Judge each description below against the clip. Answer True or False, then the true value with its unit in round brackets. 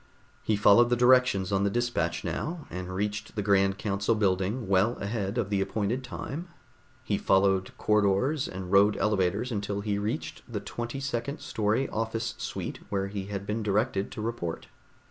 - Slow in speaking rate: False (165 wpm)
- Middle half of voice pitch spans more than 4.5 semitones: False (3.2 semitones)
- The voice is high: False (105 Hz)